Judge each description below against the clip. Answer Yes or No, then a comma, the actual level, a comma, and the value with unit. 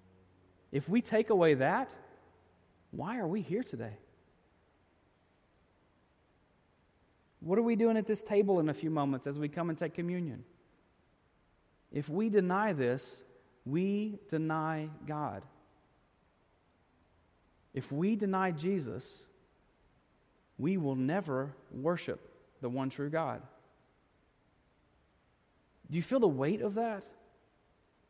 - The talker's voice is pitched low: No, medium, 150 Hz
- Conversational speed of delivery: No, slow, 115 wpm